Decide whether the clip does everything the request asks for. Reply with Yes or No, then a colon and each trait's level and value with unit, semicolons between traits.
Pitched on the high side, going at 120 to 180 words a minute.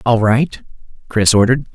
No: low, 120 Hz; average, 140 wpm